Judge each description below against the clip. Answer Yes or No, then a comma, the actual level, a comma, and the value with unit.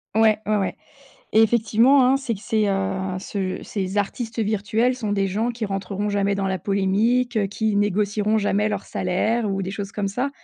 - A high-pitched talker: Yes, high, 205 Hz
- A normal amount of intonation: No, narrow, 2.2 semitones